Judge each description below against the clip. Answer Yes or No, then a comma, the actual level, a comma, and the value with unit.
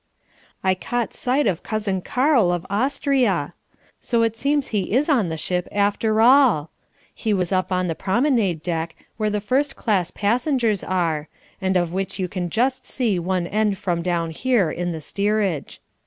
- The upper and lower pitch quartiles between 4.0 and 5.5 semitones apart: Yes, average, 5.1 semitones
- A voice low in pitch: No, high, 200 Hz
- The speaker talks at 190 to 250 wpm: No, average, 170 wpm